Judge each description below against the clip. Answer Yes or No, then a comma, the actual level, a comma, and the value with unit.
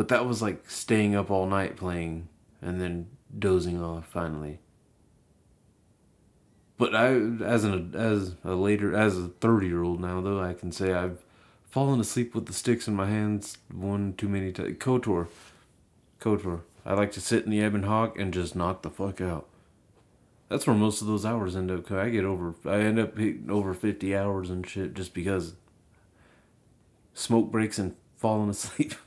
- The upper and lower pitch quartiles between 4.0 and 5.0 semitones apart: No, average, 3.2 semitones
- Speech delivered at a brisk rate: No, average, 180 wpm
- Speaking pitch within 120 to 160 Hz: No, low, 100 Hz